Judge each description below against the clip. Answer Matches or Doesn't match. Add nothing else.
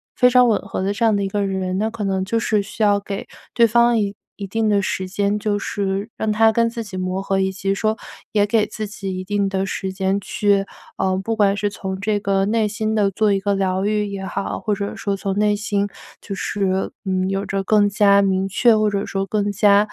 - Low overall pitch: Doesn't match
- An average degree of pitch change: Doesn't match